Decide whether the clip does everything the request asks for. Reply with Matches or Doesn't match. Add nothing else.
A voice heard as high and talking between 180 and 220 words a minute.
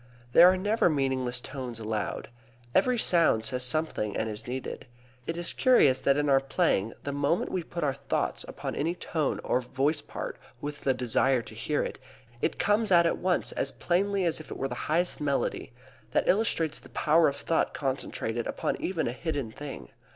Doesn't match